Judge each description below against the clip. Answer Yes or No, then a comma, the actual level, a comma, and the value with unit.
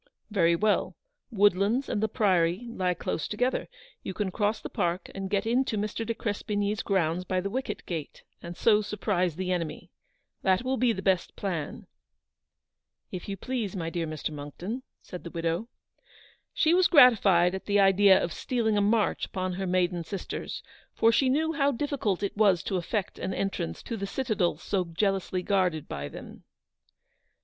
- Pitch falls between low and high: No, high, 195 Hz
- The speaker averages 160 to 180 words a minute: Yes, average, 175 wpm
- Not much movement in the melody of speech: No, average, 3.6 semitones